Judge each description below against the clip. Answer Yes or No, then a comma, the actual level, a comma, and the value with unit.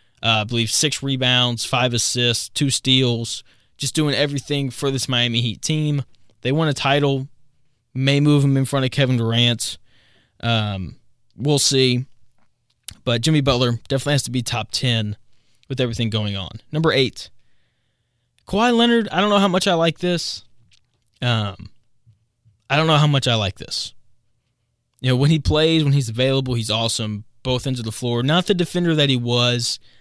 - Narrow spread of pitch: No, average, 3.4 semitones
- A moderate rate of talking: Yes, average, 175 wpm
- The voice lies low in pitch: Yes, low, 125 Hz